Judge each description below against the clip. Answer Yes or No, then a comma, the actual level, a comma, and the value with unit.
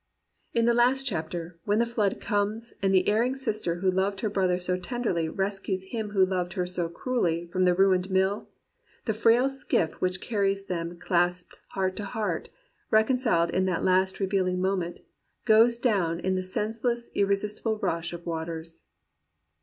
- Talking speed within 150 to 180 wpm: Yes, average, 160 wpm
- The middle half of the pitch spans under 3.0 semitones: No, average, 3.3 semitones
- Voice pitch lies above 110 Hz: Yes, high, 190 Hz